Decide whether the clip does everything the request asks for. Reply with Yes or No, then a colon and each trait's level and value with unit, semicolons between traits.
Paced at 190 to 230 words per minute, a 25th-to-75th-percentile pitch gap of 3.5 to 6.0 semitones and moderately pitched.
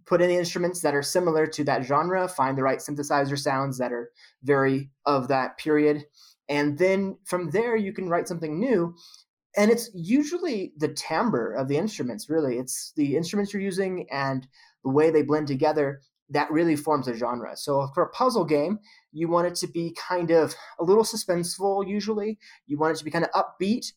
Yes: average, 200 wpm; average, 4.9 semitones; medium, 165 Hz